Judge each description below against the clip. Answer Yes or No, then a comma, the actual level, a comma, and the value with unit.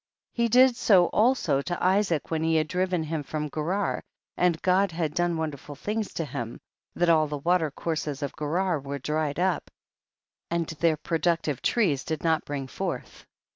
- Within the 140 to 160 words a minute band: No, average, 180 wpm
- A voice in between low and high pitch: Yes, medium, 165 Hz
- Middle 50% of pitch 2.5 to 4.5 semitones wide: Yes, average, 3.3 semitones